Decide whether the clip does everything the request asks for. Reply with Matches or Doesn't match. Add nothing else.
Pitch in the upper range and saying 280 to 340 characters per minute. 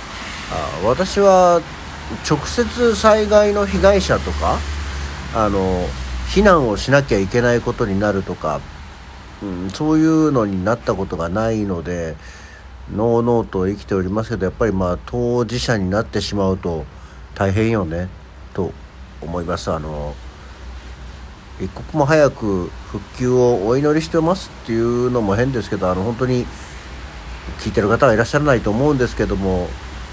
Doesn't match